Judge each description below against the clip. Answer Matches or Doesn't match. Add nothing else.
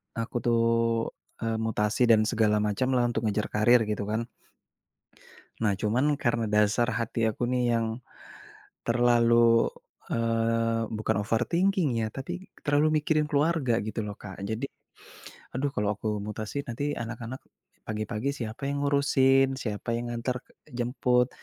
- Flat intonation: Doesn't match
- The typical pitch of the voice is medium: Doesn't match